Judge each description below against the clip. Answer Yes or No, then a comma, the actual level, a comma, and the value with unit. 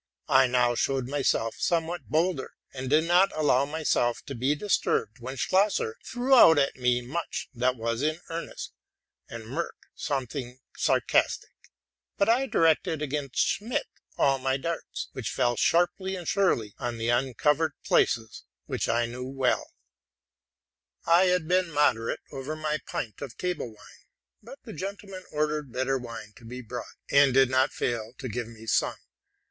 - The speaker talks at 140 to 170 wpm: Yes, average, 155 wpm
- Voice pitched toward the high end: No, low, 135 Hz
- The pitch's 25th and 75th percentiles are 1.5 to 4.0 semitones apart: No, average, 5.1 semitones